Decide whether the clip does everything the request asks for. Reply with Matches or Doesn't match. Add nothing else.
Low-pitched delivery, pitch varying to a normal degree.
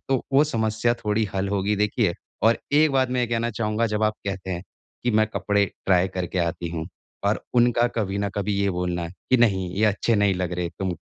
Matches